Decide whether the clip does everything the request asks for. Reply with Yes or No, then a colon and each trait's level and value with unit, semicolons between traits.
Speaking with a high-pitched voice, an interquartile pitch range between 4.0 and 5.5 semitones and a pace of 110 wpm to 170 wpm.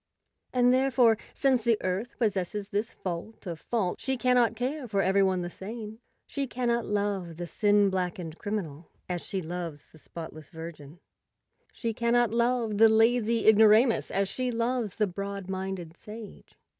Yes: high, 210 Hz; average, 4.3 semitones; average, 160 wpm